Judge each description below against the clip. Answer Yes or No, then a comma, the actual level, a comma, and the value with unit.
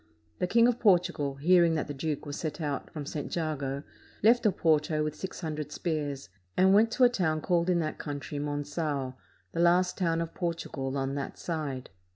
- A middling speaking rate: Yes, average, 190 wpm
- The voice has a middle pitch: Yes, medium, 155 Hz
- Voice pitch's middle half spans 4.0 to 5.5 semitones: No, average, 3.5 semitones